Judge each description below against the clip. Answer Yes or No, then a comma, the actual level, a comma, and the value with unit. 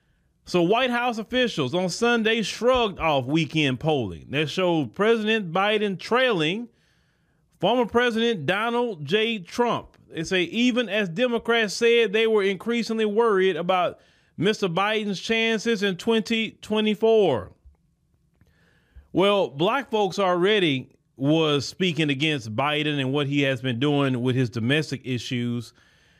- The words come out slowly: Yes, slow, 125 wpm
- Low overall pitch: No, high, 190 Hz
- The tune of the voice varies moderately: No, wide, 7.0 semitones